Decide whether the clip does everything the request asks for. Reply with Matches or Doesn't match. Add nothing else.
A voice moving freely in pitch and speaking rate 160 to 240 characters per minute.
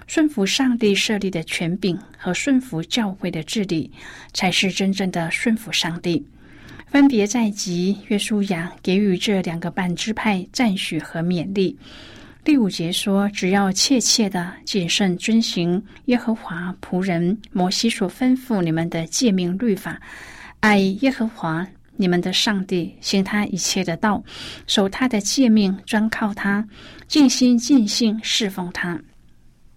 Doesn't match